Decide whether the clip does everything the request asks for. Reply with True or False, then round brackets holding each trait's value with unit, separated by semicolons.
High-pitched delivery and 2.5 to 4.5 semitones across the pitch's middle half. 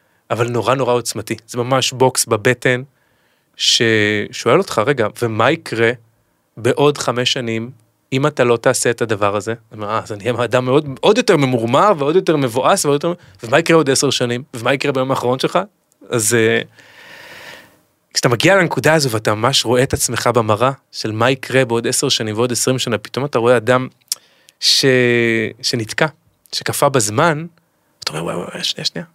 False (125 Hz; 3.3 semitones)